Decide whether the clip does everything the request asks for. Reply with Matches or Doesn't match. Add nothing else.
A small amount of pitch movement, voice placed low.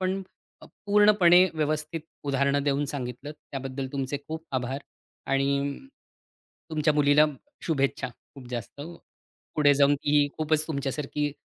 Doesn't match